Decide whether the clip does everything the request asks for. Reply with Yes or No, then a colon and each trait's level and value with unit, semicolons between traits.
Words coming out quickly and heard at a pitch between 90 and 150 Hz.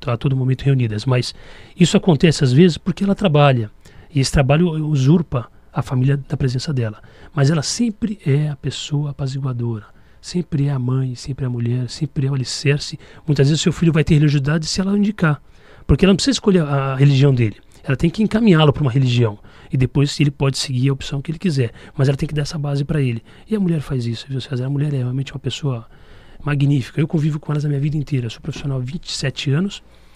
Yes: fast, 225 wpm; medium, 140 Hz